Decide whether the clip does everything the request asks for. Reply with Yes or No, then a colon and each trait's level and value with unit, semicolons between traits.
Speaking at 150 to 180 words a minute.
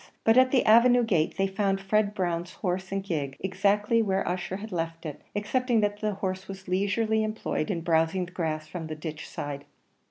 No: average, 195 wpm